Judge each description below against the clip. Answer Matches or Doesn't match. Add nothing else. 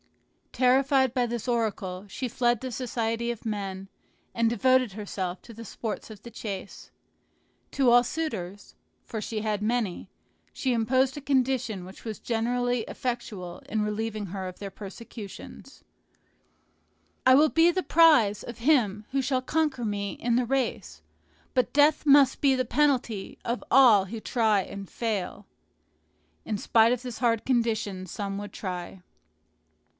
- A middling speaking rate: Matches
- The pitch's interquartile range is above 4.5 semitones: Doesn't match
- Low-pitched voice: Doesn't match